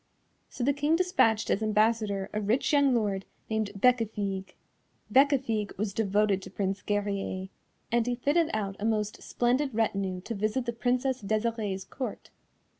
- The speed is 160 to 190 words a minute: No, average, 150 wpm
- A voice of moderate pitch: No, high, 220 Hz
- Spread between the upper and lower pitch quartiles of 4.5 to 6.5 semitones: No, average, 3.5 semitones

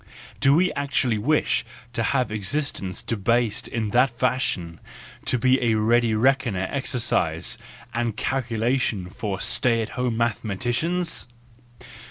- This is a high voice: No, low, 120 Hz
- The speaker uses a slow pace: Yes, slow, 120 wpm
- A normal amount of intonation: Yes, average, 3.2 semitones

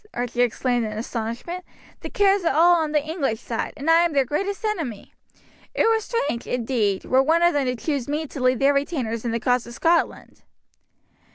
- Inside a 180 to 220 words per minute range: Yes, average, 200 wpm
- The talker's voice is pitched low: No, very high, 275 Hz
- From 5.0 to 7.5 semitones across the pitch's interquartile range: Yes, wide, 5.6 semitones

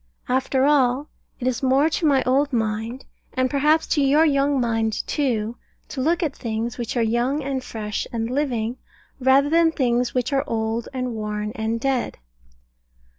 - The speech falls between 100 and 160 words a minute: No, average, 170 wpm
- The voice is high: Yes, very high, 255 Hz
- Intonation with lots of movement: No, average, 3.4 semitones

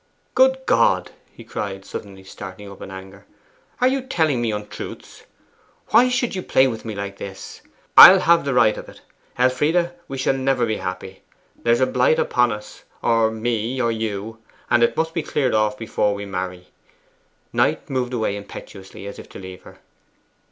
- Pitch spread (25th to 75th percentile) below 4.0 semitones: No, average, 5.1 semitones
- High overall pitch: No, low, 115 Hz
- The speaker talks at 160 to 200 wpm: Yes, average, 180 wpm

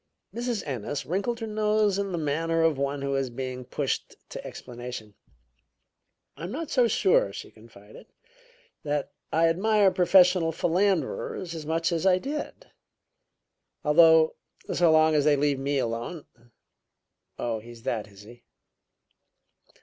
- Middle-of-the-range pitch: Yes, medium, 160 Hz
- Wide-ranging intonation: Yes, wide, 6.0 semitones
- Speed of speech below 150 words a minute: Yes, average, 140 wpm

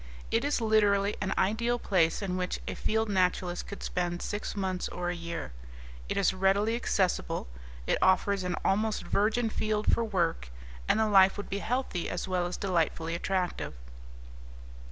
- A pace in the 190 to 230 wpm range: No, average, 165 wpm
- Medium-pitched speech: No, high, 195 Hz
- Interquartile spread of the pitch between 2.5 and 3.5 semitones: Yes, average, 3.0 semitones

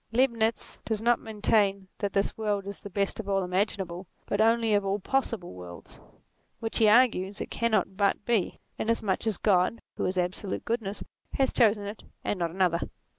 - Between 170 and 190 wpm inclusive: Yes, average, 175 wpm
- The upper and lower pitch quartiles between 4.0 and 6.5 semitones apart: No, average, 2.8 semitones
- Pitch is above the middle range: Yes, high, 205 Hz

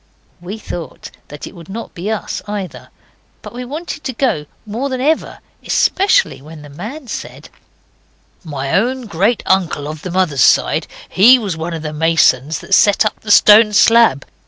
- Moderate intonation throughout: No, wide, 6.6 semitones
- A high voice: Yes, high, 195 Hz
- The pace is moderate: Yes, average, 175 wpm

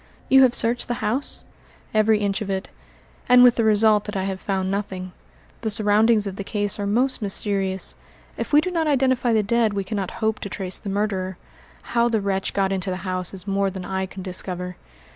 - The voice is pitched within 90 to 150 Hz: No, high, 205 Hz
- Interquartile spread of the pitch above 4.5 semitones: No, average, 2.9 semitones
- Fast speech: Yes, fast, 210 wpm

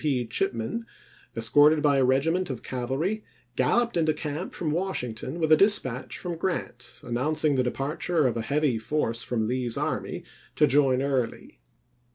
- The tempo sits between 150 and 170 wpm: Yes, average, 155 wpm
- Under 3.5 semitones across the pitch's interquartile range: No, average, 4.3 semitones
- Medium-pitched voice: Yes, medium, 145 Hz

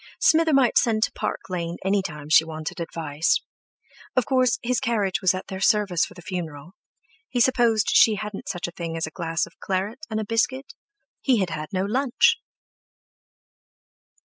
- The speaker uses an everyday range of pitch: No, wide, 5.9 semitones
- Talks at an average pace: Yes, average, 170 wpm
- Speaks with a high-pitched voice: Yes, high, 195 Hz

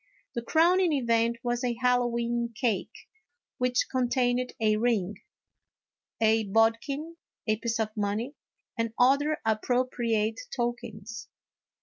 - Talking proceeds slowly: Yes, slow, 110 wpm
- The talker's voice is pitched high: Yes, high, 235 Hz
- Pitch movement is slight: Yes, narrow, 2.0 semitones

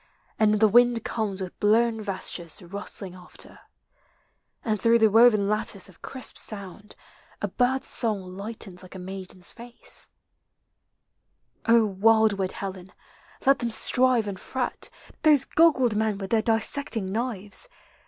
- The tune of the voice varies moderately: Yes, average, 3.3 semitones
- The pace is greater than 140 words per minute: No, slow, 135 wpm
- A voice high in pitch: Yes, high, 215 Hz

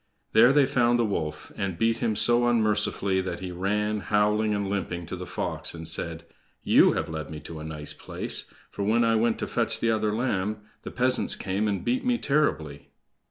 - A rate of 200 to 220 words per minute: Yes, fast, 205 wpm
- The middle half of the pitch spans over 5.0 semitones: No, average, 4.5 semitones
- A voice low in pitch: Yes, low, 105 Hz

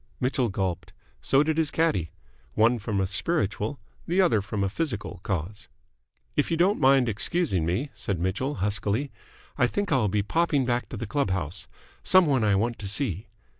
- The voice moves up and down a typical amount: No, wide, 6.7 semitones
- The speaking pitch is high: No, low, 110 Hz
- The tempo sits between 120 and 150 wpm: No, average, 175 wpm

